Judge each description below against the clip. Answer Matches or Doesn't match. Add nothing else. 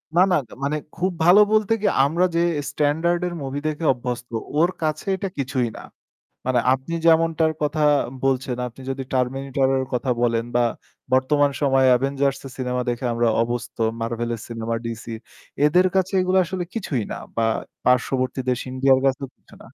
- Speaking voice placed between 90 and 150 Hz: Matches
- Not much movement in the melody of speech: Doesn't match